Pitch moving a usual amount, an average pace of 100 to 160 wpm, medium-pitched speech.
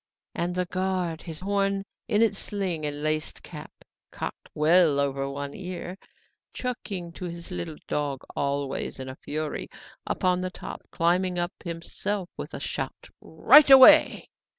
Yes: average, 3.6 semitones; average, 145 wpm; medium, 175 Hz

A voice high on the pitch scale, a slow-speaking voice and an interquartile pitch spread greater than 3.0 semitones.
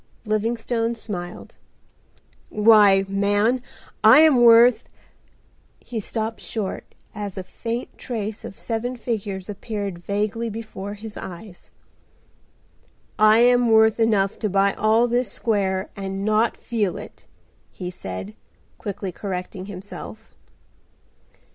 No: high, 215 Hz; slow, 110 wpm; narrow, 2.6 semitones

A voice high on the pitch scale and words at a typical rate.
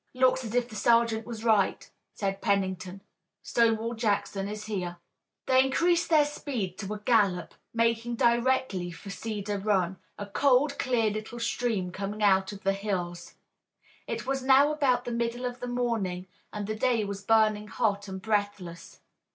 Yes: high, 215 Hz; average, 160 wpm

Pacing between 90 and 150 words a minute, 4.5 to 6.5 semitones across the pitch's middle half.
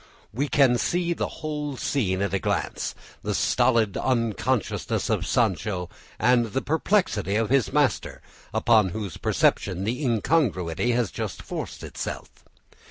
Yes: slow, 135 wpm; average, 5.3 semitones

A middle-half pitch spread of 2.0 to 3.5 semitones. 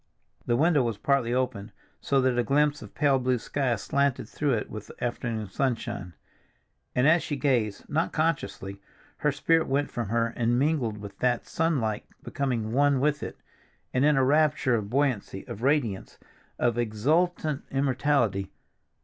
No: average, 3.9 semitones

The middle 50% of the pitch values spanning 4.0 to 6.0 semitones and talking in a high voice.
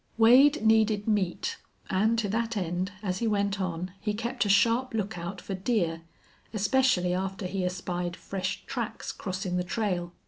No: average, 3.6 semitones; high, 195 Hz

